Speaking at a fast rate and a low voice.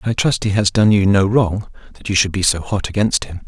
Yes: fast, 275 wpm; low, 100 Hz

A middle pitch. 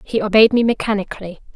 No: high, 210 Hz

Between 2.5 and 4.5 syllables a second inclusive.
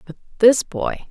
Yes: 4.2 syllables/s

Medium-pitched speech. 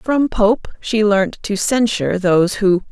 No: high, 210 Hz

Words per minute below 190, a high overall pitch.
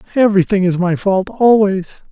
Yes: average, 140 wpm; high, 195 Hz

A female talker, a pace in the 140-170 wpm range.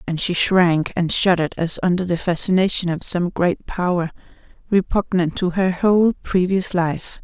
Yes: female; average, 155 wpm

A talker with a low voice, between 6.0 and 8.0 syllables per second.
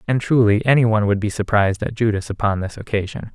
Yes: low, 110 Hz; 6.6 syllables/s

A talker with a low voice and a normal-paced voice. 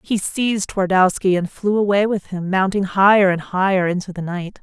No: high, 190 Hz; average, 195 wpm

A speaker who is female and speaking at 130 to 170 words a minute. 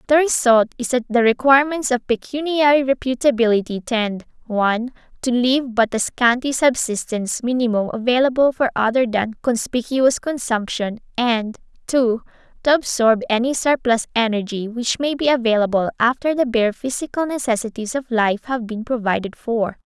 Yes: female; average, 140 wpm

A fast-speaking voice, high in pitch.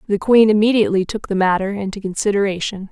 No: average, 165 wpm; high, 205 Hz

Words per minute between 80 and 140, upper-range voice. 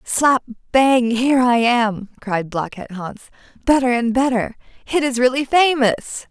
Yes: slow, 135 wpm; high, 245 Hz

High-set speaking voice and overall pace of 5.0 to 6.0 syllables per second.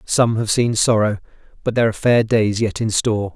No: low, 110 Hz; 5.7 syllables/s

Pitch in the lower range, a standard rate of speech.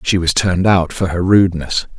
No: very low, 90 Hz; fast, 210 wpm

